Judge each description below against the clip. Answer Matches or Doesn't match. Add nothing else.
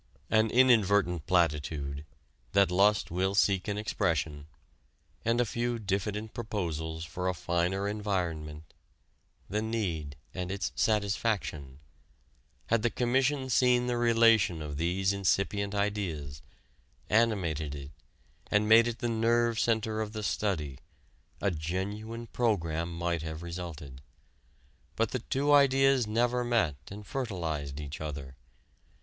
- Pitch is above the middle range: Doesn't match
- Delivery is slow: Matches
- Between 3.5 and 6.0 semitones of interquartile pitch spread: Matches